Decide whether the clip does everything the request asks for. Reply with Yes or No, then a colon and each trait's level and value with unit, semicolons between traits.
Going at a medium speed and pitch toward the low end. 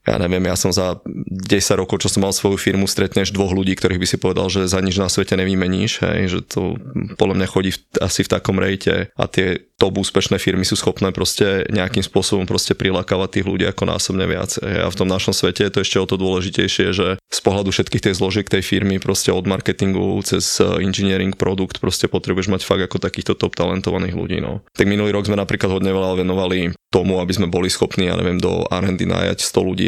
No: fast, 220 wpm; very low, 95 Hz